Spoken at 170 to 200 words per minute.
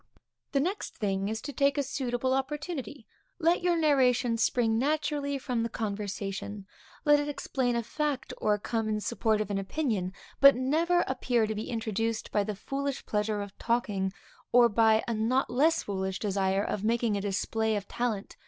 Yes: average, 180 wpm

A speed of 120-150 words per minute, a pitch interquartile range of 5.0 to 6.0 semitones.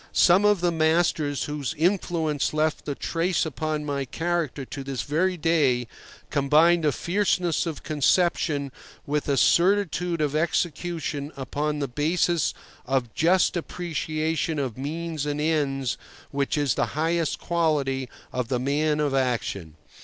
No: average, 140 wpm; average, 3.2 semitones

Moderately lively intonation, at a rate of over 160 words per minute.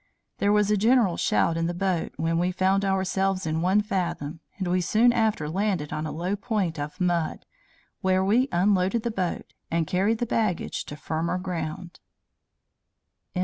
Yes: average, 3.5 semitones; average, 170 wpm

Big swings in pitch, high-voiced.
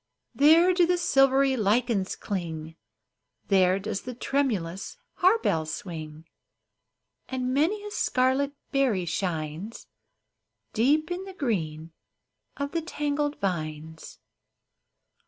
Yes: wide, 8.9 semitones; high, 240 Hz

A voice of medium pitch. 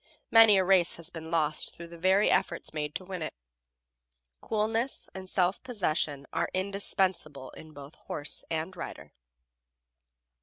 Yes: medium, 175 Hz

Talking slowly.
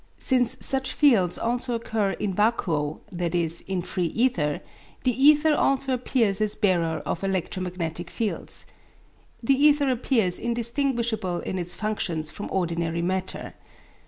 Yes: slow, 130 wpm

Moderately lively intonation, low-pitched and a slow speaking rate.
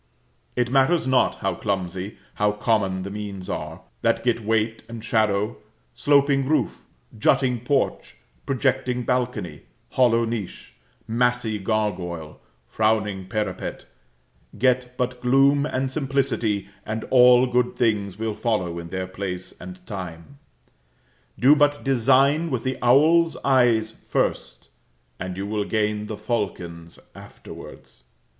Yes: average, 4.3 semitones; low, 115 Hz; slow, 125 wpm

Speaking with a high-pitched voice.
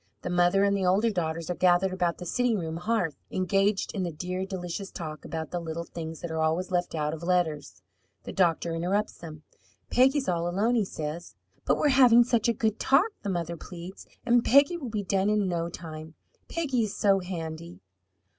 No: medium, 180 Hz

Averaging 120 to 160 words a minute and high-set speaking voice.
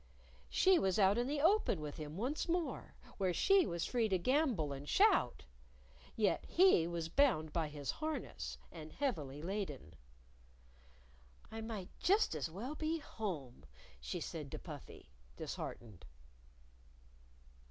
Yes: slow, 135 wpm; high, 195 Hz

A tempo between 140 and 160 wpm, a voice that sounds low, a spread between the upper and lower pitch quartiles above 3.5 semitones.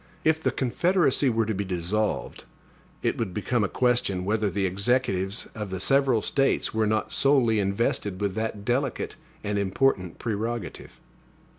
Yes: average, 150 wpm; low, 110 Hz; average, 4.0 semitones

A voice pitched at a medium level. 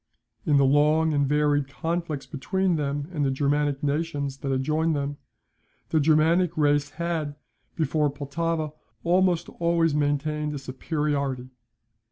Yes: medium, 150 Hz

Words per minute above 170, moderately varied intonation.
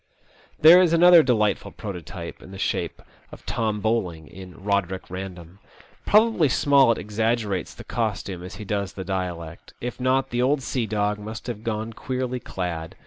No: average, 160 wpm; average, 4.9 semitones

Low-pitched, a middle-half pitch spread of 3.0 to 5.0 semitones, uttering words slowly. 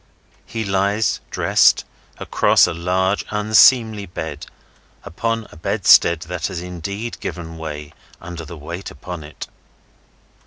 Yes: very low, 90 Hz; average, 3.9 semitones; slow, 120 wpm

